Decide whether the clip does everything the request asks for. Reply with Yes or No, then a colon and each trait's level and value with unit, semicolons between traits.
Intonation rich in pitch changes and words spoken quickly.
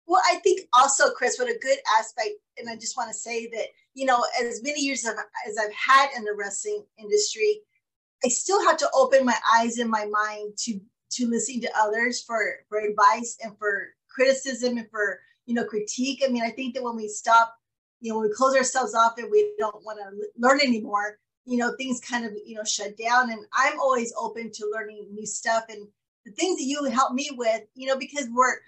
No: average, 3.7 semitones; fast, 220 wpm